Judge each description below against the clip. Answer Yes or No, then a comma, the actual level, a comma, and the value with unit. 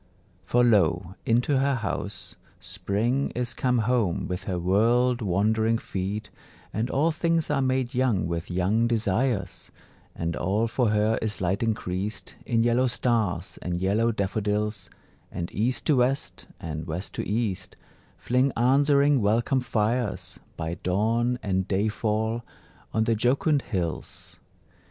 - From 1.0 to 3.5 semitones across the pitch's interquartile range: No, average, 4.2 semitones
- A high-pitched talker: No, low, 110 Hz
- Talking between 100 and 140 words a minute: Yes, slow, 135 wpm